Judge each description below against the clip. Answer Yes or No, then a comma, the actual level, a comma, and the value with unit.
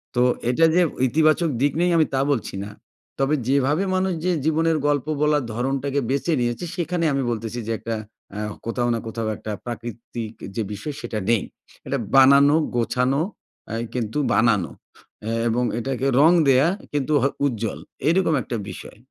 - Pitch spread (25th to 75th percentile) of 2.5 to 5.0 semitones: Yes, average, 4.5 semitones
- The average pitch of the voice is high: No, low, 135 Hz